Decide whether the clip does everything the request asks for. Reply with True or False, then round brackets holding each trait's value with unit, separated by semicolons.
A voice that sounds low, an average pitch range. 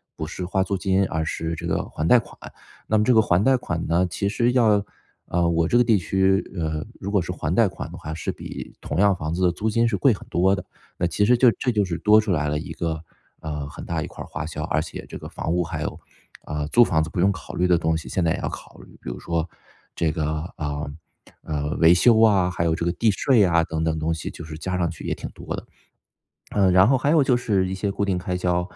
True (90 Hz; 4.0 semitones)